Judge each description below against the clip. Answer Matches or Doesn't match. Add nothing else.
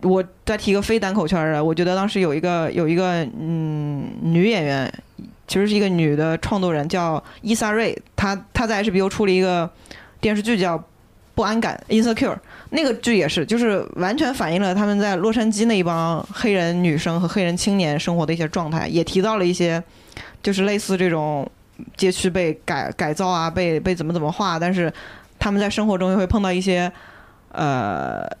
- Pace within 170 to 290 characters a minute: Doesn't match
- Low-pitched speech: Doesn't match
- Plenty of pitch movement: Doesn't match